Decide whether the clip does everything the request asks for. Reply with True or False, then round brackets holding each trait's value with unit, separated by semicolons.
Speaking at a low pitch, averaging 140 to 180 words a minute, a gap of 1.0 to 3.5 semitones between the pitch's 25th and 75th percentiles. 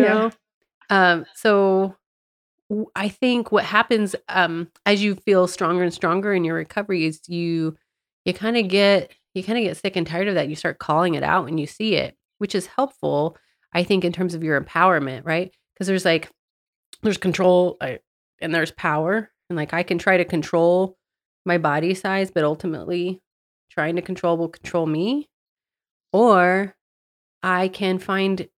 False (180 Hz; 175 wpm; 3.0 semitones)